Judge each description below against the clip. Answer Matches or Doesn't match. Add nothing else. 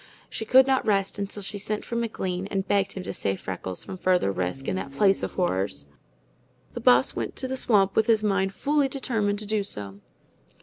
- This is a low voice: Doesn't match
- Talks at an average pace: Doesn't match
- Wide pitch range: Matches